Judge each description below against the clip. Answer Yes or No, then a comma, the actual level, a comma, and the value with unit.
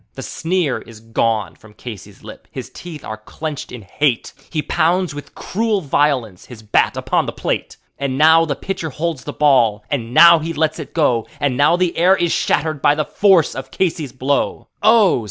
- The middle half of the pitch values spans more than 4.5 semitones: Yes, average, 5.3 semitones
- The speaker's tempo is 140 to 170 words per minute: No, average, 190 wpm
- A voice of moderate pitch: Yes, medium, 145 Hz